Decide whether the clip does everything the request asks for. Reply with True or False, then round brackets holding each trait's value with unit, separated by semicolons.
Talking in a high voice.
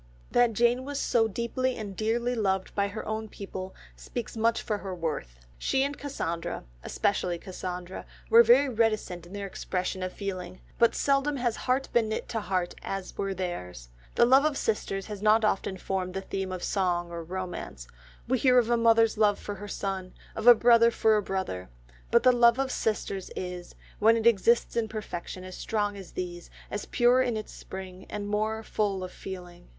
True (205 Hz)